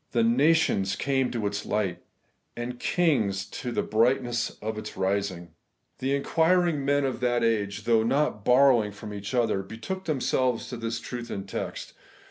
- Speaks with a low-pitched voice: Yes, low, 115 Hz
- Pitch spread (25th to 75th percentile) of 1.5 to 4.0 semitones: No, average, 4.5 semitones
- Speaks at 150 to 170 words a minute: Yes, average, 165 wpm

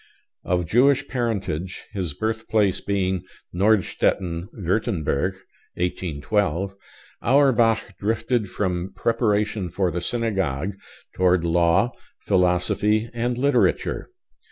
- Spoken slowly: Yes, slow, 85 wpm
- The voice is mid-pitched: No, low, 100 Hz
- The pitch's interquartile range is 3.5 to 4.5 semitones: Yes, average, 4.1 semitones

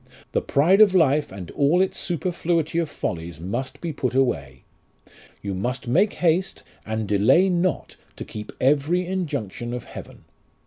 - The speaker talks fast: No, average, 150 wpm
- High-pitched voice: No, medium, 140 Hz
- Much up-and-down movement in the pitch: Yes, wide, 8.1 semitones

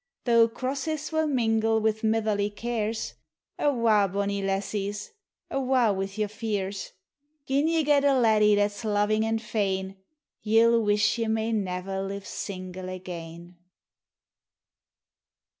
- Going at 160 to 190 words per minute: No, slow, 135 wpm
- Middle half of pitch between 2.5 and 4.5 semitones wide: Yes, average, 2.8 semitones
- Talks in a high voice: Yes, high, 215 Hz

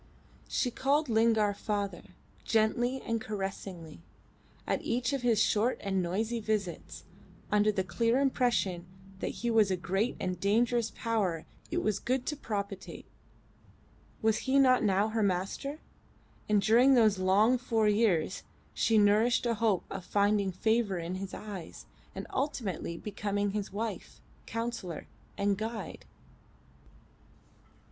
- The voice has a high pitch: Yes, high, 215 Hz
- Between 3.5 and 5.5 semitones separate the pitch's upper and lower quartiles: No, average, 3.1 semitones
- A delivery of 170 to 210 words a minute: No, slow, 135 wpm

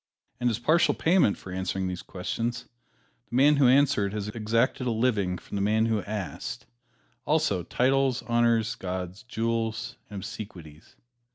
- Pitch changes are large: No, average, 3.8 semitones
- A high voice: No, low, 110 Hz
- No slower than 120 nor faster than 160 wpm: Yes, average, 150 wpm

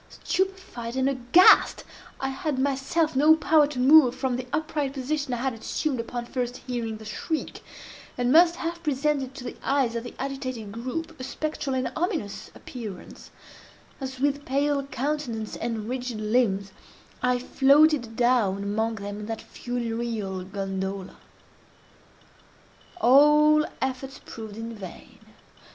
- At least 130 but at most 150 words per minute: Yes, average, 140 wpm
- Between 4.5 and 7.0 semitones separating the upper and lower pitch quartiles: No, average, 4.1 semitones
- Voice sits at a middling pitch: No, very high, 255 Hz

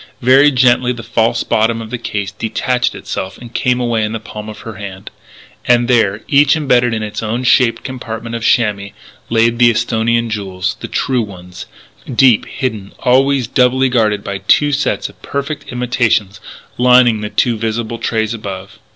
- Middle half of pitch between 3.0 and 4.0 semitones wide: No, narrow, 2.6 semitones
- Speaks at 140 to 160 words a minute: No, average, 170 wpm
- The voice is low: Yes, low, 115 Hz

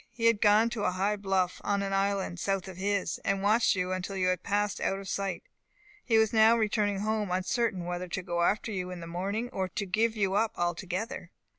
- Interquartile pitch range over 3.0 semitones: No, narrow, 2.6 semitones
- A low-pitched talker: No, high, 195 Hz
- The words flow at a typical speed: No, fast, 225 wpm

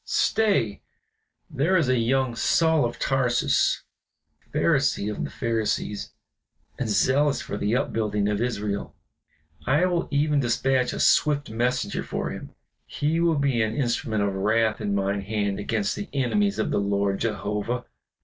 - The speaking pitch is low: Yes, low, 120 Hz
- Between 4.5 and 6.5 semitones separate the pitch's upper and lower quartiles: Yes, average, 5.2 semitones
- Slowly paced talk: No, average, 150 wpm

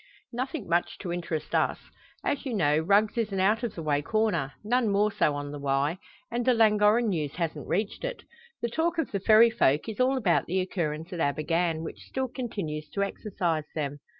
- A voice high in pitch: Yes, high, 195 Hz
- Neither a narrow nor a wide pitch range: No, wide, 6.3 semitones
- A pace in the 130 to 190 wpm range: No, fast, 205 wpm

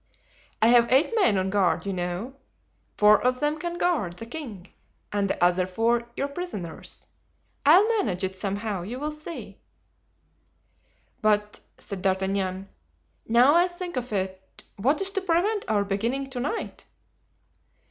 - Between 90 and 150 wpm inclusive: Yes, average, 145 wpm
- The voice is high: Yes, high, 230 Hz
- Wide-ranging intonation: Yes, wide, 7.7 semitones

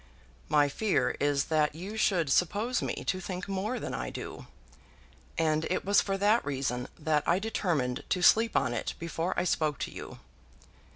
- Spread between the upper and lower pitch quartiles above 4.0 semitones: Yes, average, 5.1 semitones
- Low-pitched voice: No, medium, 175 Hz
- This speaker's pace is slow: No, average, 175 wpm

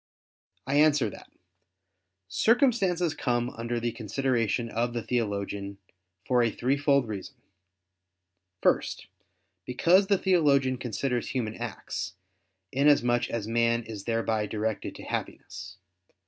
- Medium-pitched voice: No, low, 120 Hz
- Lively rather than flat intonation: No, average, 3.8 semitones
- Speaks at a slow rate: Yes, slow, 110 wpm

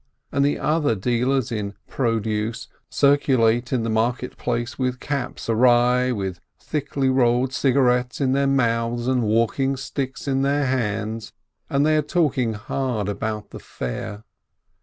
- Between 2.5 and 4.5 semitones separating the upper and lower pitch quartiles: Yes, average, 3.2 semitones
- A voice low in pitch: Yes, low, 125 Hz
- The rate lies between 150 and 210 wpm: No, average, 140 wpm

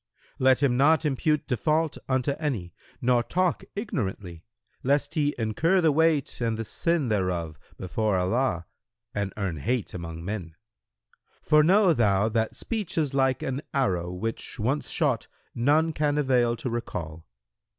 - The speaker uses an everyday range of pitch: No, wide, 7.2 semitones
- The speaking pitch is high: No, low, 125 Hz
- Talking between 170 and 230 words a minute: No, average, 145 wpm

